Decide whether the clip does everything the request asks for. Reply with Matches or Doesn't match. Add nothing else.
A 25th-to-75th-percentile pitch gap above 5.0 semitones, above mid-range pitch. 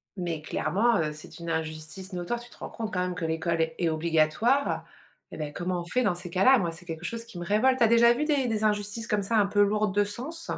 Matches